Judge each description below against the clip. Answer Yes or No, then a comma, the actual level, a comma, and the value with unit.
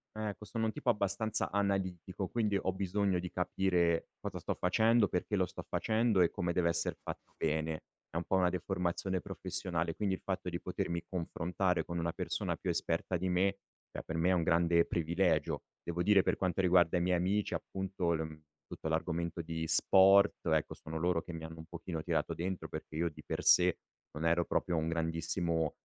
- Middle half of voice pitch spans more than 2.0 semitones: Yes, narrow, 2.5 semitones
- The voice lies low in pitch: Yes, very low, 90 Hz